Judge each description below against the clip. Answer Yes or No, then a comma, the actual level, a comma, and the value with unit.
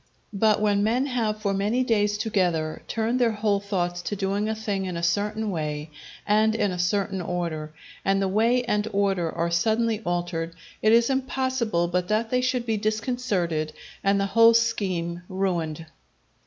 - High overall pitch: Yes, high, 205 Hz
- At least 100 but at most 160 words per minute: No, average, 170 wpm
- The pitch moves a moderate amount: Yes, average, 4.1 semitones